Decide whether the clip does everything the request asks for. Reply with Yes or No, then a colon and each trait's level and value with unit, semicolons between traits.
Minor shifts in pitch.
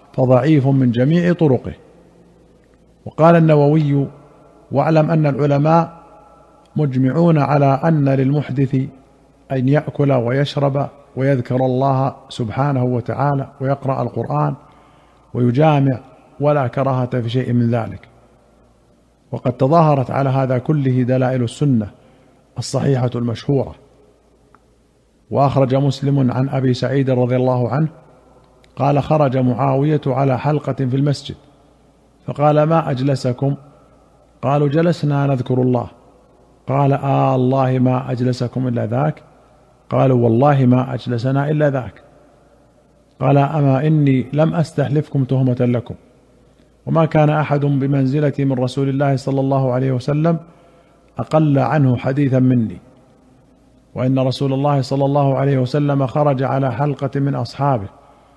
Yes: narrow, 2.3 semitones